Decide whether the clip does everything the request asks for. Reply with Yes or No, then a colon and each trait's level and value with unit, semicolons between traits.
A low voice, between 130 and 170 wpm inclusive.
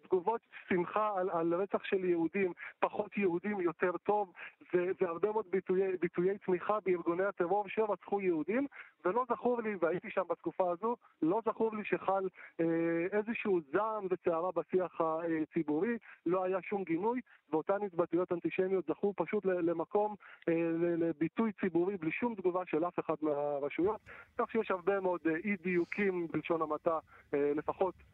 No: medium, 185 Hz; average, 145 wpm